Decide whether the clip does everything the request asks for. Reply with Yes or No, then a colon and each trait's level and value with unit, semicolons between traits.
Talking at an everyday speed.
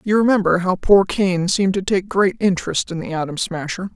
No: fast, 215 wpm